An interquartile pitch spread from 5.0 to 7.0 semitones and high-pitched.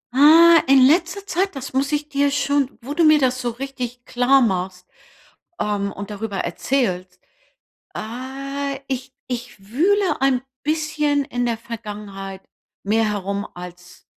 Yes: wide, 5.5 semitones; very high, 255 Hz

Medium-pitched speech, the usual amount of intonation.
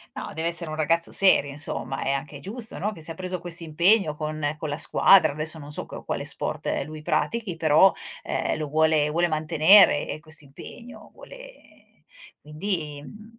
Yes: medium, 160 Hz; average, 3.6 semitones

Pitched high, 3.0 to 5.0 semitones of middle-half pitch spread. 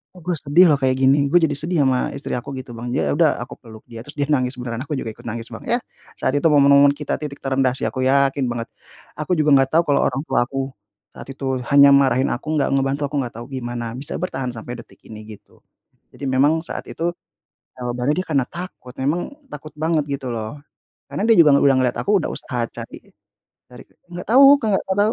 No: medium, 140 Hz; average, 3.4 semitones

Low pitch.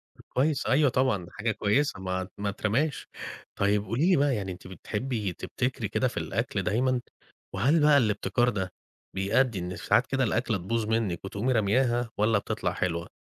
Yes: low, 110 Hz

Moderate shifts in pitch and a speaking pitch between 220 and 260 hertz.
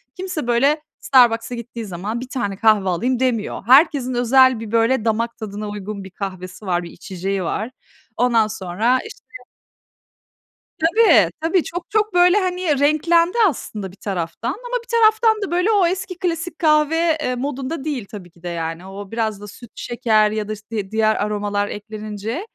No: wide, 7.2 semitones; high, 235 Hz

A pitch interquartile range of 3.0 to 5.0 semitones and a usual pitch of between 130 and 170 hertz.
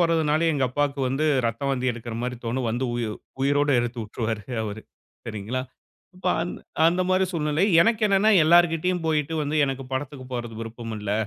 No: wide, 5.4 semitones; low, 135 Hz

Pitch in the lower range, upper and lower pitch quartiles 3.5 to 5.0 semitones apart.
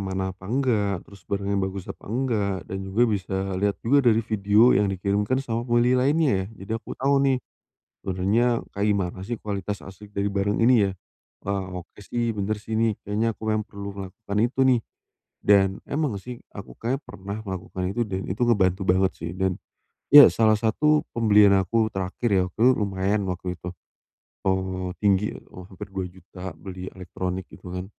No: low, 100 Hz; average, 3.1 semitones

